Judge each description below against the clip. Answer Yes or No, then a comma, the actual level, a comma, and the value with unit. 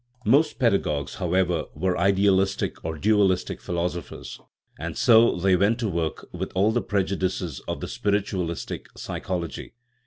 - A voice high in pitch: No, very low, 95 Hz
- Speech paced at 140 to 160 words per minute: Yes, average, 145 wpm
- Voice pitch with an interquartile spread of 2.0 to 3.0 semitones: Yes, average, 2.7 semitones